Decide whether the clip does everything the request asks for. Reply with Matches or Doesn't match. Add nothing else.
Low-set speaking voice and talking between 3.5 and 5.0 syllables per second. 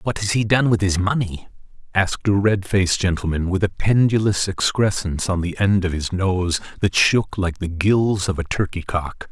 Matches